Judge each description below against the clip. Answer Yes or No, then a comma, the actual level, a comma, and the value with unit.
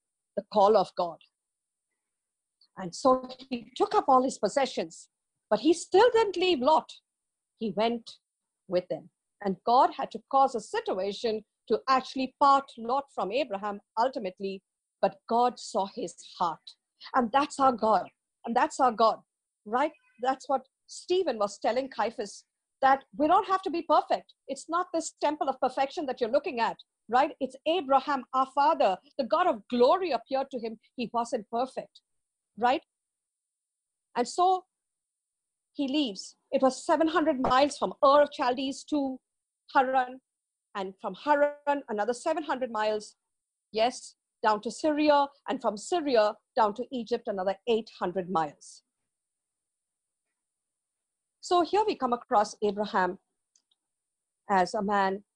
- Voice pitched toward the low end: No, very high, 255 Hz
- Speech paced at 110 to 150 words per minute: Yes, average, 140 wpm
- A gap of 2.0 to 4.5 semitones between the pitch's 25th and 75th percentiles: No, average, 5.1 semitones